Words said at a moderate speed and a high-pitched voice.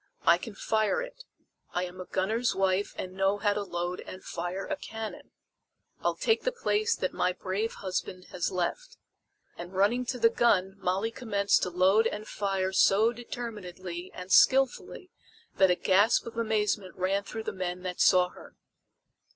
Yes: average, 170 wpm; high, 195 Hz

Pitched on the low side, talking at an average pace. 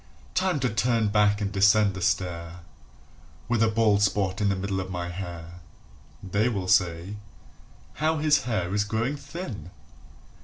Yes: low, 100 Hz; average, 155 wpm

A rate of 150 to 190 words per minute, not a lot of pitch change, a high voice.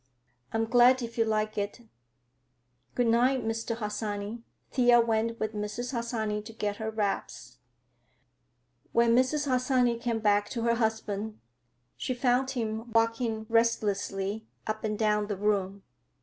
No: slow, 135 wpm; narrow, 2.2 semitones; high, 225 Hz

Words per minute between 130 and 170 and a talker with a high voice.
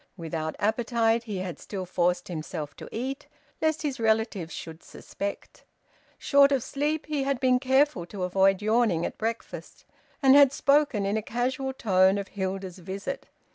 Yes: average, 160 wpm; high, 220 Hz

